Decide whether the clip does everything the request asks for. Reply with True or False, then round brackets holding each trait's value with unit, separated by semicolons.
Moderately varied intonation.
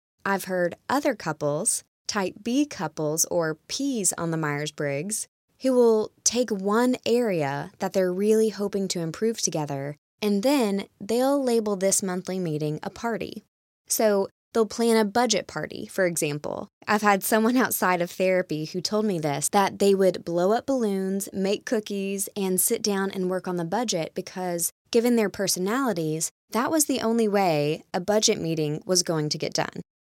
True (4.5 semitones)